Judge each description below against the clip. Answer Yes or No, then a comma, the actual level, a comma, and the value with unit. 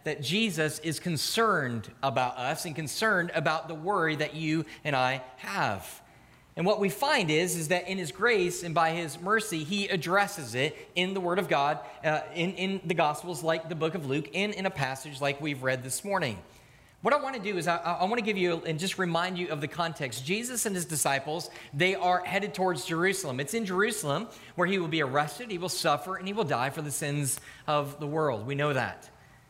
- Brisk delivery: Yes, fast, 220 wpm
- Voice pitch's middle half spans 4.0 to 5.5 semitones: Yes, average, 4.4 semitones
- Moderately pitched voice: Yes, medium, 165 Hz